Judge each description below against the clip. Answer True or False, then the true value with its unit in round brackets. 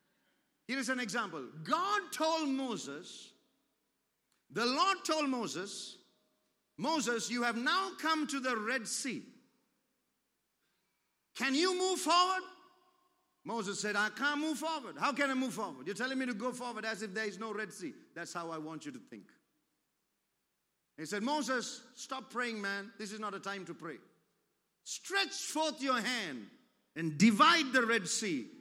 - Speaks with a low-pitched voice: False (255 Hz)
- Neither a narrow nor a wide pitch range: False (5.7 semitones)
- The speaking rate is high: False (160 wpm)